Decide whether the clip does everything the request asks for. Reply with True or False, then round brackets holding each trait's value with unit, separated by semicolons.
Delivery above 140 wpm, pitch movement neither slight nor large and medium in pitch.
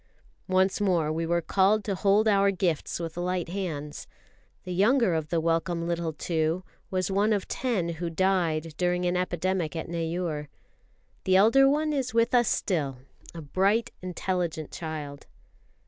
True (155 wpm; 3.2 semitones; 180 Hz)